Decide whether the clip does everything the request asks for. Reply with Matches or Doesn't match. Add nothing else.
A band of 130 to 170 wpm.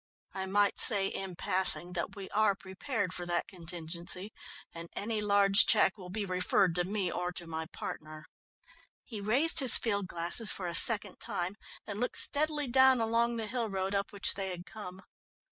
Doesn't match